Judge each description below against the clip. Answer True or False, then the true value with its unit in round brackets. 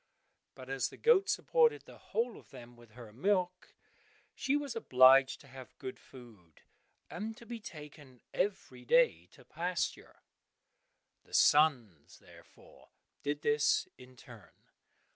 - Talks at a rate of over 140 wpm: False (135 wpm)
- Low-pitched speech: False (145 Hz)